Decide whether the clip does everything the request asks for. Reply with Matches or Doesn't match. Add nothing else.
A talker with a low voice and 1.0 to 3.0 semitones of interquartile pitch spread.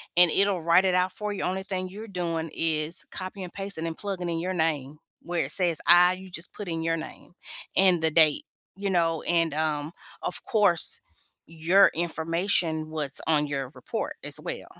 Doesn't match